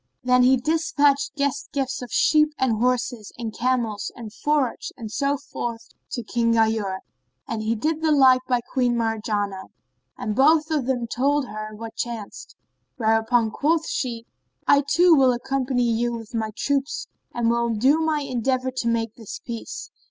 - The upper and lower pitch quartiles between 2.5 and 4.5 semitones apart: Yes, average, 3.5 semitones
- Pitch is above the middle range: Yes, high, 245 Hz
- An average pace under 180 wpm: Yes, average, 160 wpm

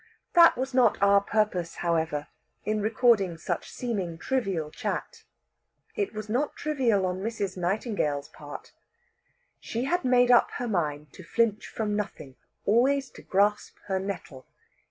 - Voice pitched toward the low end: No, high, 210 Hz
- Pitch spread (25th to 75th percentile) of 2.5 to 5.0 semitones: No, wide, 5.4 semitones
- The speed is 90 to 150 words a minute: Yes, average, 140 wpm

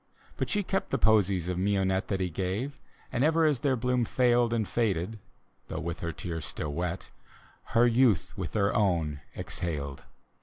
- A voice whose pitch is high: No, low, 100 Hz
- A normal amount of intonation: No, wide, 5.7 semitones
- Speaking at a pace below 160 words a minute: No, average, 175 wpm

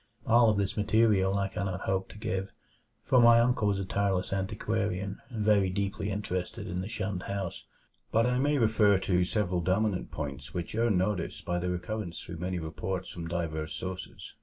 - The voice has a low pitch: Yes, very low, 95 Hz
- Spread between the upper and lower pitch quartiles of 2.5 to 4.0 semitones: Yes, average, 2.9 semitones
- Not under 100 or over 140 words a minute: No, average, 185 wpm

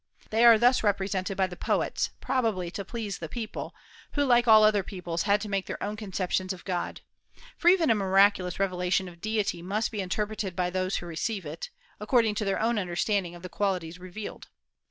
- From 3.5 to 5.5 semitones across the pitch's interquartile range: No, average, 3.0 semitones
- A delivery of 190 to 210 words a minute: Yes, average, 195 wpm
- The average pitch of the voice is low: No, high, 195 Hz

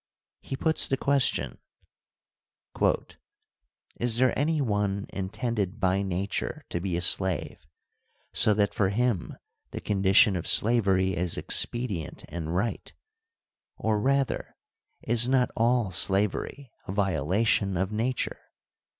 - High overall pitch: No, low, 105 Hz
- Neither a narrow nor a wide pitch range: Yes, average, 4.1 semitones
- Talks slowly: Yes, slow, 115 wpm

